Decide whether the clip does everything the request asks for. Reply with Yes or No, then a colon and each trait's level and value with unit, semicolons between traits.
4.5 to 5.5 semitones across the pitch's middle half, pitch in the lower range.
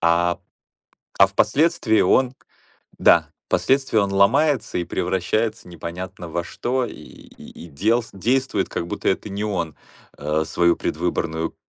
Yes: average, 5.2 semitones; very low, 95 Hz